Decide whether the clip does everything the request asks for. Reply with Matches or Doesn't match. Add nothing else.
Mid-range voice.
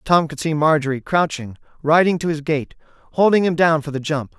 Matches